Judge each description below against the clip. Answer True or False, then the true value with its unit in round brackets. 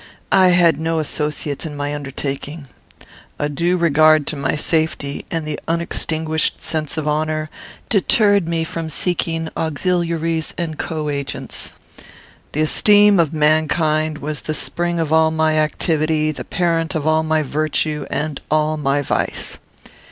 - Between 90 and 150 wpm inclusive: True (145 wpm)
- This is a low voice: False (155 Hz)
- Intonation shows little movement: True (1.5 semitones)